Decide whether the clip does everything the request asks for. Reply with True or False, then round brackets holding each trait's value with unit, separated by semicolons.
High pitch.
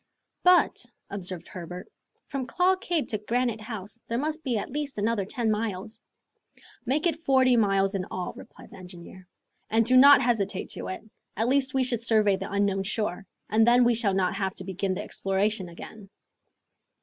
True (220 Hz)